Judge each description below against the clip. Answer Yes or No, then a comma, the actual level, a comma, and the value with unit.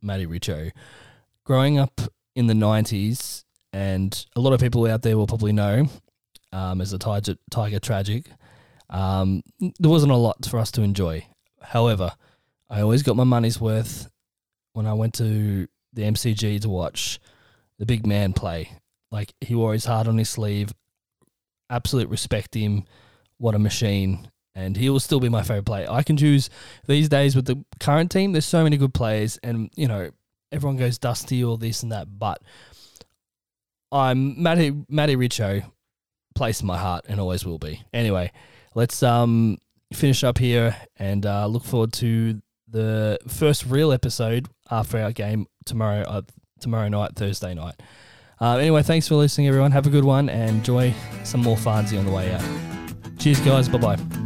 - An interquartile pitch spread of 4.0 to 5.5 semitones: No, average, 3.6 semitones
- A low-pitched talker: Yes, low, 115 Hz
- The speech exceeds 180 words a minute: No, average, 175 wpm